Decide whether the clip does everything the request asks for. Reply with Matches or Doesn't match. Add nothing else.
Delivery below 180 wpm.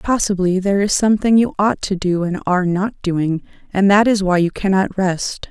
Doesn't match